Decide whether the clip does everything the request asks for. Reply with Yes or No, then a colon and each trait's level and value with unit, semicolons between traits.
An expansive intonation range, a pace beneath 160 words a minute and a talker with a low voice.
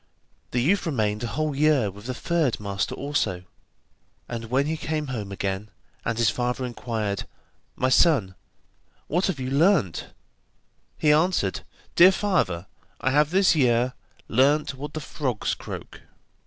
Yes: wide, 5.8 semitones; average, 145 wpm; low, 130 Hz